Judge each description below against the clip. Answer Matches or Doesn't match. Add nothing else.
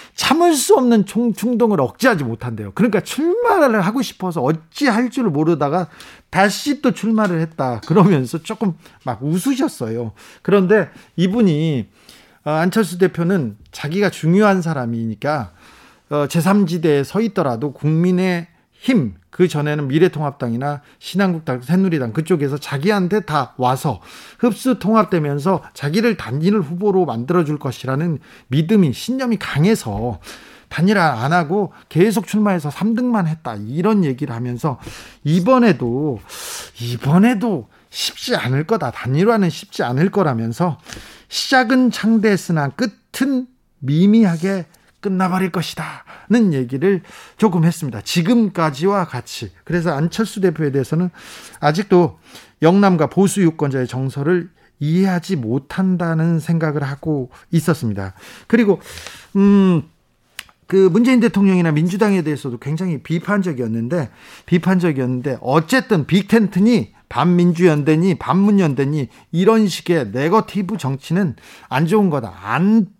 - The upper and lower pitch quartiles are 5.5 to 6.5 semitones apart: Matches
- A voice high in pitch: Doesn't match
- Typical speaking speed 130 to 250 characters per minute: Doesn't match